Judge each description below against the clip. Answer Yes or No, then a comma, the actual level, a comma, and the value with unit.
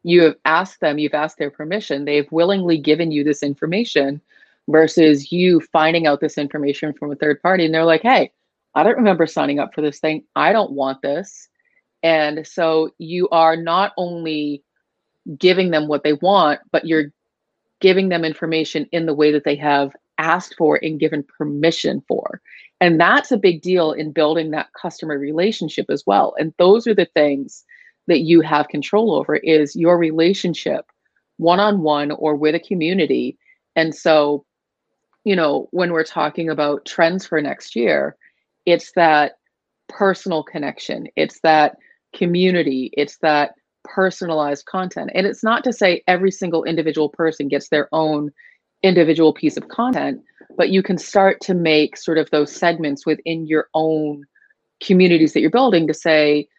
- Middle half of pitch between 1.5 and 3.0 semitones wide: Yes, average, 2.7 semitones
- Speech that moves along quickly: No, average, 170 wpm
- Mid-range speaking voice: Yes, medium, 160 Hz